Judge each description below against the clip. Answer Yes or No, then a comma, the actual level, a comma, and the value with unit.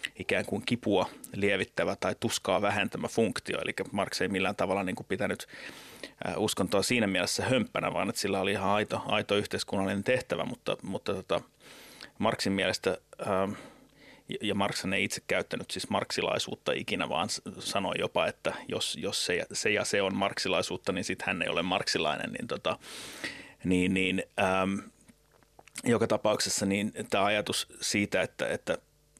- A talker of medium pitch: No, low, 100 Hz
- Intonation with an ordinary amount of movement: No, narrow, 1.4 semitones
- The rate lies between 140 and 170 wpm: Yes, average, 150 wpm